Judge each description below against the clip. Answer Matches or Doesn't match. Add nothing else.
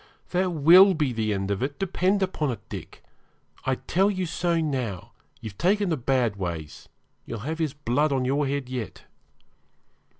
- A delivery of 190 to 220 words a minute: Doesn't match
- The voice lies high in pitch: Doesn't match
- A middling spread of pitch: Doesn't match